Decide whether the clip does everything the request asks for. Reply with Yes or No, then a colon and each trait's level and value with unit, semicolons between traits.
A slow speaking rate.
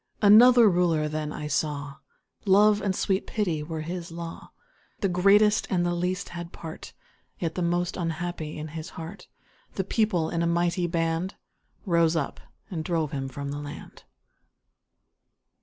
No: average, 155 wpm